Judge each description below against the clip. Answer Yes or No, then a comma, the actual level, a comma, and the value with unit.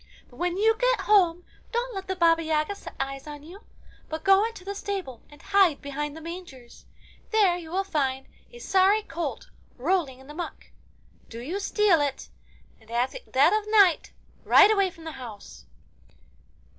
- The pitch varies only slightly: No, wide, 5.4 semitones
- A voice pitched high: Yes, very high, 345 Hz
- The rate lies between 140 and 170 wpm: No, average, 180 wpm